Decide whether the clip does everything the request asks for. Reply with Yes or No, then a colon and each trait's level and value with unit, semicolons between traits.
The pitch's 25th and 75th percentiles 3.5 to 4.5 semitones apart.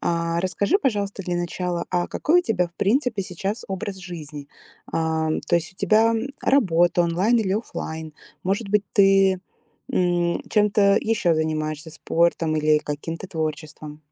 Yes: average, 3.8 semitones